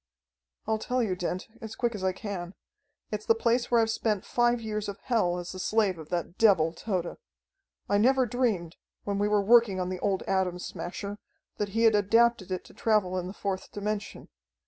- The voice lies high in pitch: Yes, high, 205 Hz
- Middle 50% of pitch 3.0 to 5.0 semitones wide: Yes, average, 3.4 semitones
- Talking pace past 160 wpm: Yes, average, 200 wpm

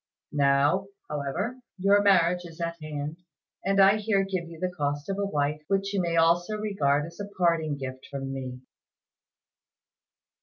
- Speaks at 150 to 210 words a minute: Yes, average, 160 wpm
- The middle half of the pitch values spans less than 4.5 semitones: No, average, 5.1 semitones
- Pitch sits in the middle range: Yes, medium, 170 Hz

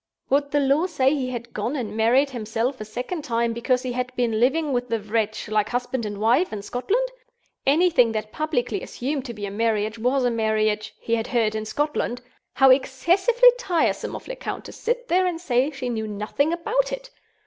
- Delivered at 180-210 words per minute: Yes, average, 200 wpm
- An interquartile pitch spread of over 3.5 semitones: Yes, average, 5.1 semitones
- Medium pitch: No, very high, 250 Hz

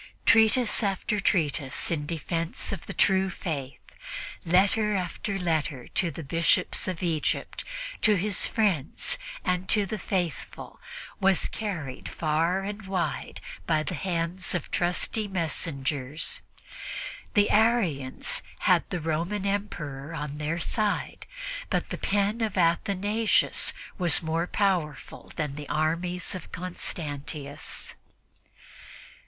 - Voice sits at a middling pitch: Yes, medium, 175 Hz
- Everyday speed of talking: No, slow, 115 wpm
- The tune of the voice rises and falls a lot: No, average, 4.3 semitones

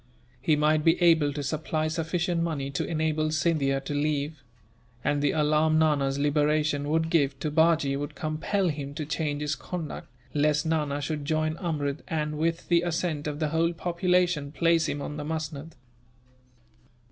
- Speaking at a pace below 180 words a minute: Yes, average, 165 wpm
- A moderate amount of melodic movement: No, narrow, 1.9 semitones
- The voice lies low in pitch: No, medium, 155 Hz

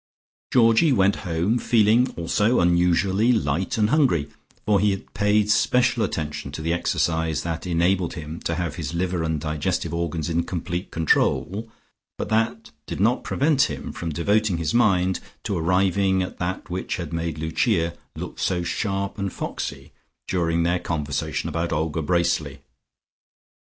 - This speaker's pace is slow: No, average, 150 wpm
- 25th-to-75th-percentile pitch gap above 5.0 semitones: No, average, 3.8 semitones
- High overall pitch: No, very low, 90 Hz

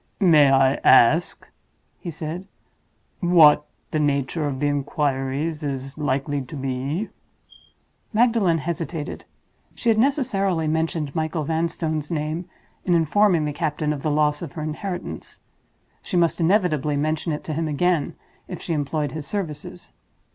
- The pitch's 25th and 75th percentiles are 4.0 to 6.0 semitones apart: No, average, 2.9 semitones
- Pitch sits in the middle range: Yes, medium, 155 Hz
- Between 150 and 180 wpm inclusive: No, average, 140 wpm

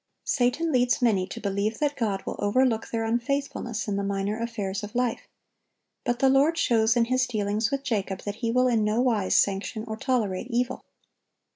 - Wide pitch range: No, average, 3.4 semitones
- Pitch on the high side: Yes, high, 230 Hz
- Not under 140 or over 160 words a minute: No, average, 185 wpm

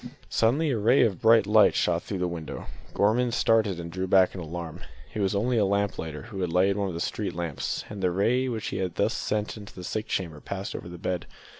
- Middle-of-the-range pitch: No, low, 100 Hz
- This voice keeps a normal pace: No, fast, 245 wpm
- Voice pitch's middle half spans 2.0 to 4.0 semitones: Yes, average, 3.7 semitones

